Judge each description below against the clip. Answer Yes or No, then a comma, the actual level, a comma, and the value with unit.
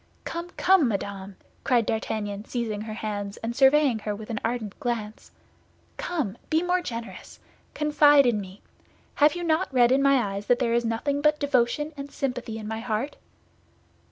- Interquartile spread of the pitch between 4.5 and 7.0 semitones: Yes, average, 5.1 semitones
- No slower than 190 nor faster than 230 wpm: No, average, 170 wpm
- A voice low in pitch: No, high, 240 Hz